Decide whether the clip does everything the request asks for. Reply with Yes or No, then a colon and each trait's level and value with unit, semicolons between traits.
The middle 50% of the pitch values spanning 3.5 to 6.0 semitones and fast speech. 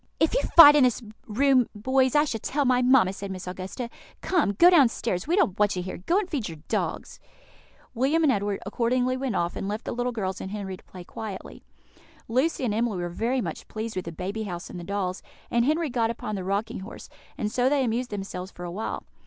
Yes: average, 5.2 semitones; fast, 225 wpm